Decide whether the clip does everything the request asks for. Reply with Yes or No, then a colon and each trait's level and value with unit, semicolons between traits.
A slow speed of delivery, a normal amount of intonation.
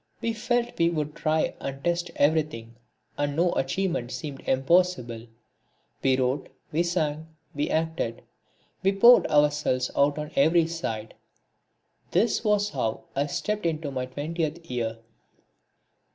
Yes: slow, 130 wpm; average, 4.4 semitones